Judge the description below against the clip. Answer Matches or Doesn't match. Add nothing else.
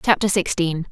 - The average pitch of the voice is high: Doesn't match